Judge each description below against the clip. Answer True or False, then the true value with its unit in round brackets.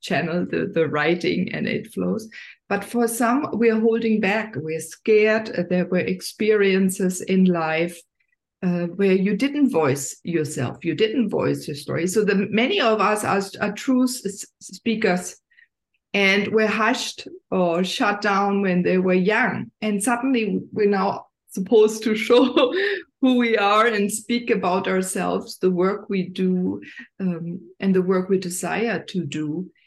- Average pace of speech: True (155 wpm)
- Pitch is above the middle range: True (200 Hz)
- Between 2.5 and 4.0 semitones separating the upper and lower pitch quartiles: True (3.7 semitones)